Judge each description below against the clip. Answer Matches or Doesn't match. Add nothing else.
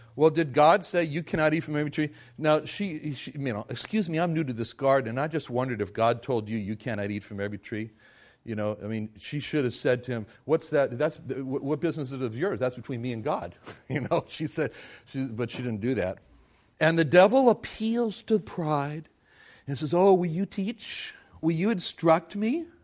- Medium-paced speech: Doesn't match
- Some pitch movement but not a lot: Doesn't match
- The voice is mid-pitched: Matches